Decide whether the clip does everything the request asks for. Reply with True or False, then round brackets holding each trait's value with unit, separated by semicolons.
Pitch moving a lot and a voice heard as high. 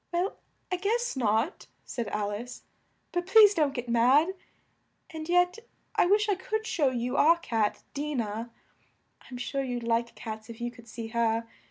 True (7.3 semitones; 255 Hz)